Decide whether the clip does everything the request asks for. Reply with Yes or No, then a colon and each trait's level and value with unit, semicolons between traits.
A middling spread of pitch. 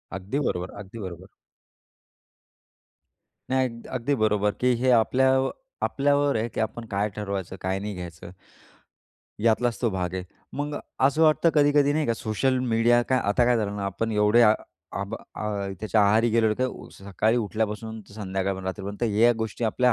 Yes: average, 3.8 semitones